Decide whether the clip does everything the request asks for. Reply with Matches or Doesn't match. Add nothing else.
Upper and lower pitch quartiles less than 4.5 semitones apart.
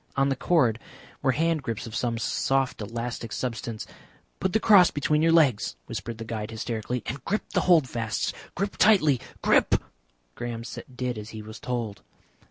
Doesn't match